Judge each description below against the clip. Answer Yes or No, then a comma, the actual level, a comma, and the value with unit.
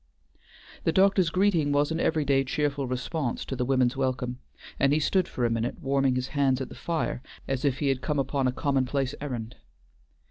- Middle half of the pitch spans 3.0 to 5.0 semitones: No, narrow, 2.5 semitones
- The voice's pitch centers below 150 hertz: Yes, low, 135 Hz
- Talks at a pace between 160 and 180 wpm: No, average, 200 wpm